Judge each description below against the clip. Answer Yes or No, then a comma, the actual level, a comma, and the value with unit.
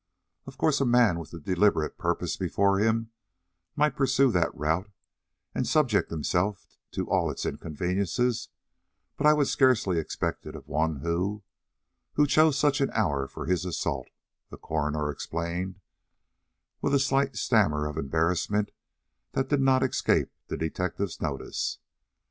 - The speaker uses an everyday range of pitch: No, wide, 8.2 semitones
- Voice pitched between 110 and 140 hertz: No, low, 100 Hz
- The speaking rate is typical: Yes, average, 145 wpm